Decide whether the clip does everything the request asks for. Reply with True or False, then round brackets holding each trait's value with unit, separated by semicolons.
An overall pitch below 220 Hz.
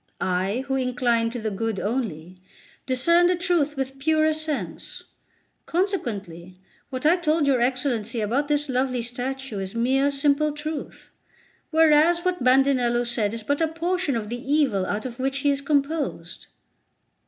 False (270 Hz)